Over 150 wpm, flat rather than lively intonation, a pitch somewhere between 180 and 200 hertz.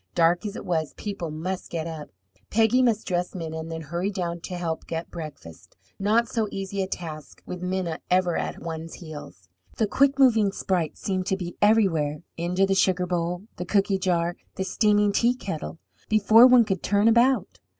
No: average, 180 wpm; average, 3.7 semitones; medium, 185 Hz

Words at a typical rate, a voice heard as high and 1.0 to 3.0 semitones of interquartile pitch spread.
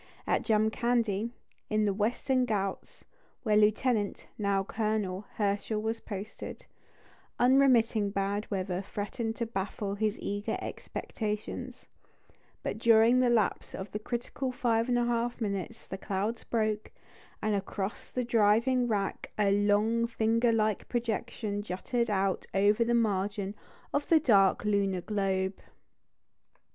No: slow, 130 wpm; high, 215 Hz; narrow, 2.6 semitones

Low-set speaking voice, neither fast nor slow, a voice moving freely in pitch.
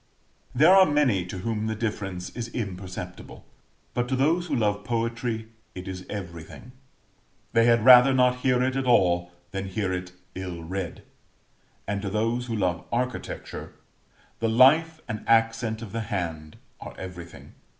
No: low, 110 Hz; average, 155 wpm; average, 4.8 semitones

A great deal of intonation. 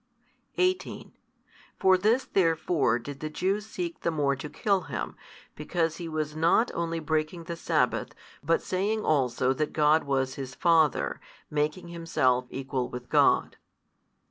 No: average, 3.9 semitones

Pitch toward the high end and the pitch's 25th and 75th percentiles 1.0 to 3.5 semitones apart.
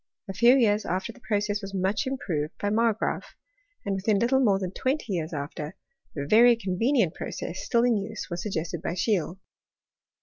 No: high, 205 Hz; average, 4.3 semitones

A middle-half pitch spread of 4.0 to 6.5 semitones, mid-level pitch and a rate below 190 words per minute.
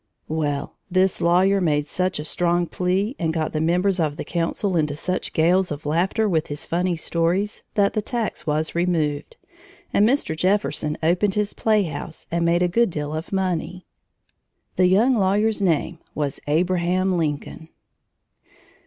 No: average, 3.3 semitones; medium, 175 Hz; average, 155 wpm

